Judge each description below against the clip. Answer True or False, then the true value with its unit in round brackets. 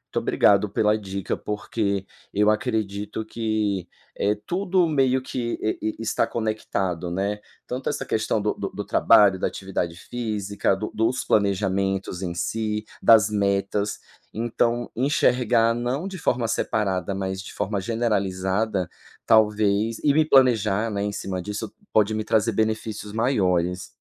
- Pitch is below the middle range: True (105 Hz)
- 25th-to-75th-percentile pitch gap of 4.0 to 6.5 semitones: False (2.7 semitones)